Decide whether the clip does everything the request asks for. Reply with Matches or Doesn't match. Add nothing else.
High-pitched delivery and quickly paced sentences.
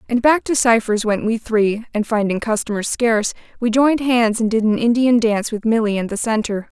Matches